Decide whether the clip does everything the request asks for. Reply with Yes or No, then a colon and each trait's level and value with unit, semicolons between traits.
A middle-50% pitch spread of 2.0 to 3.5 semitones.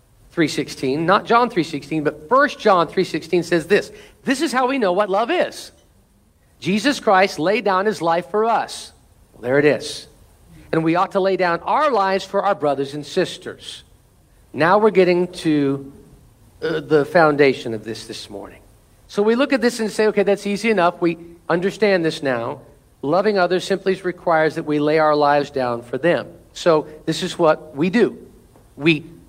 No: average, 5.1 semitones